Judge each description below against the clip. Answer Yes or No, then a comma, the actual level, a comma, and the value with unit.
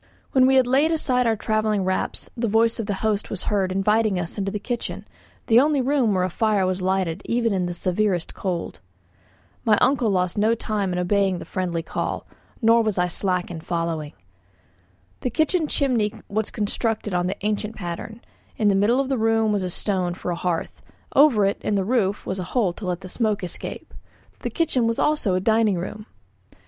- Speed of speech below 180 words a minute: No, average, 200 wpm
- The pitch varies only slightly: No, average, 3.7 semitones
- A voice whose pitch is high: Yes, high, 210 Hz